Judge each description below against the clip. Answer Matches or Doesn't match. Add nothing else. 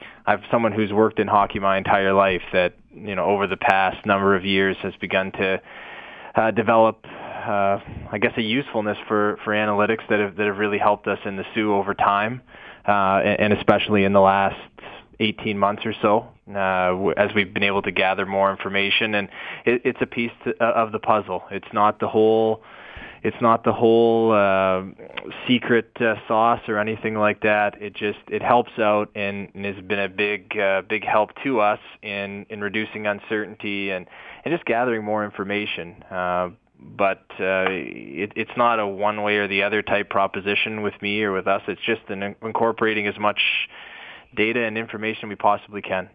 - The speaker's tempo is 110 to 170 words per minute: Doesn't match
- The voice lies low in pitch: Matches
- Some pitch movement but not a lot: Doesn't match